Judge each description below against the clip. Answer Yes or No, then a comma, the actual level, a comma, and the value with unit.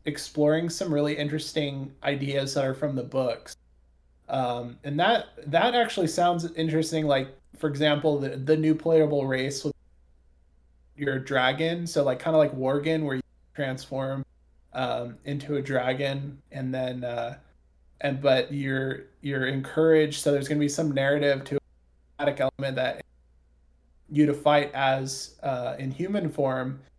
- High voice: No, medium, 140 Hz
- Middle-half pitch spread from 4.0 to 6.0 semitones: No, average, 2.7 semitones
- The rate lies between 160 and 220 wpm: No, average, 150 wpm